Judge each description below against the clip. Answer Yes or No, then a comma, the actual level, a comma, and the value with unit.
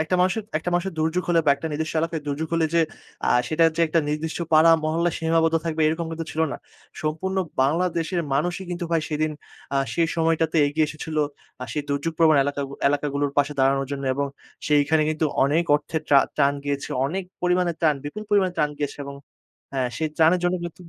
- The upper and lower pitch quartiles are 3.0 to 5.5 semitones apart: No, narrow, 2.4 semitones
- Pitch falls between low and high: Yes, medium, 160 Hz